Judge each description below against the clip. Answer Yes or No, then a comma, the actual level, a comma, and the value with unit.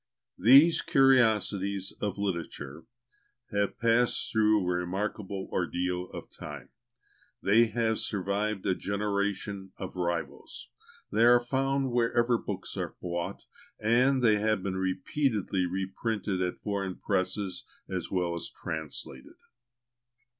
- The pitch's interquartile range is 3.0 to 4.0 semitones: Yes, average, 3.6 semitones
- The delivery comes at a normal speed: No, slow, 115 wpm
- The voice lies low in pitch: Yes, low, 100 Hz